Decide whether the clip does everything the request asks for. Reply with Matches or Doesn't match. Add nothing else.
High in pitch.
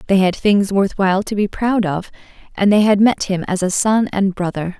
Matches